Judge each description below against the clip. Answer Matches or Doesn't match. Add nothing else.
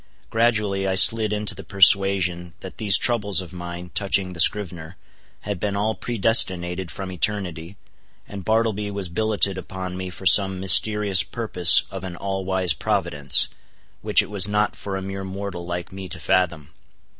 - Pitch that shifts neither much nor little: Doesn't match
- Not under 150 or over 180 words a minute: Matches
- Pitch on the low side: Matches